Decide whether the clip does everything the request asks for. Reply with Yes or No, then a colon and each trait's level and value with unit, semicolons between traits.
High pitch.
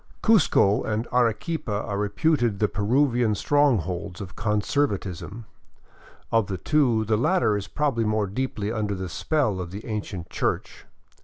No: low, 110 Hz